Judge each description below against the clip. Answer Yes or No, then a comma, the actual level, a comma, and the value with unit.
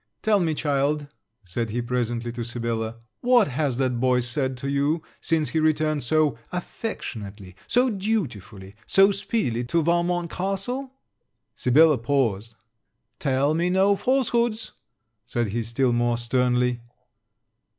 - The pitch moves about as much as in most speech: No, wide, 6.7 semitones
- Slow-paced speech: Yes, slow, 130 wpm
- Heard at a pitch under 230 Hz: Yes, medium, 140 Hz